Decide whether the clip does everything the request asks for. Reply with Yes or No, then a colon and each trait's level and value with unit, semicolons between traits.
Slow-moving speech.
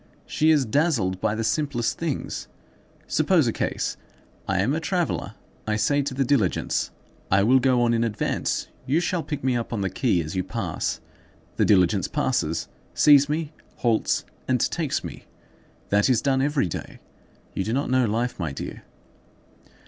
No: average, 170 wpm